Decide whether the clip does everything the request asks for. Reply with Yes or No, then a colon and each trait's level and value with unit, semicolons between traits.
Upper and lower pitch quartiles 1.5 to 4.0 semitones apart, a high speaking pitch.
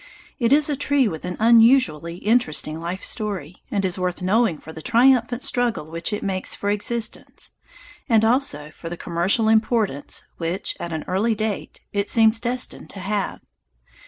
No: average, 5.2 semitones; high, 205 Hz